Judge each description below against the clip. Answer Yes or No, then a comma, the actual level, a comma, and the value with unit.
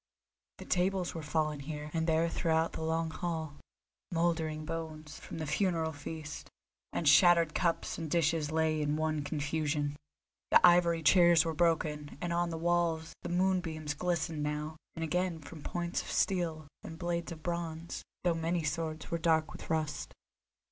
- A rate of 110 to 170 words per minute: Yes, average, 160 wpm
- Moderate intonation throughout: No, narrow, 1.7 semitones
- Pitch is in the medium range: Yes, medium, 160 Hz